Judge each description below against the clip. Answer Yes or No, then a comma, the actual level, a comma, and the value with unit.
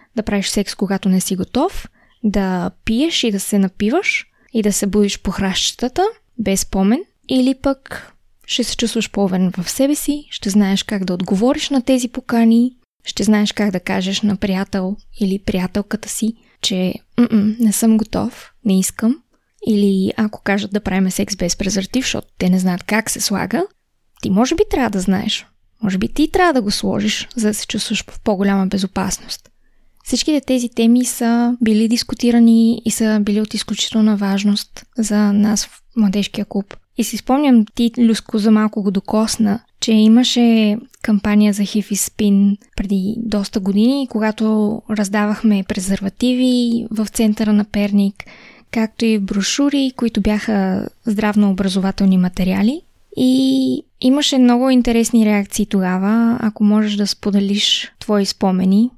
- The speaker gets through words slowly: No, average, 155 wpm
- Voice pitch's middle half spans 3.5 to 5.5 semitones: No, average, 2.9 semitones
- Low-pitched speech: No, high, 215 Hz